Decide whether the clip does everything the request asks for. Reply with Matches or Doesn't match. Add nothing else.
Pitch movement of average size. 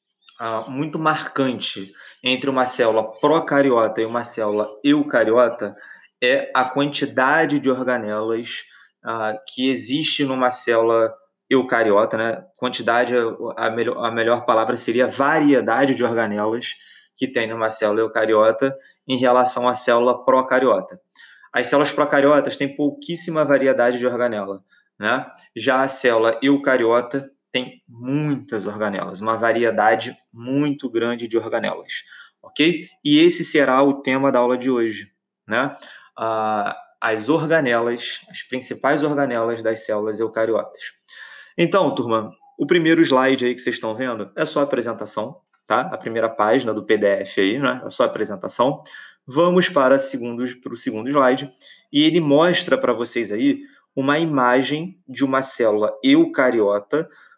Matches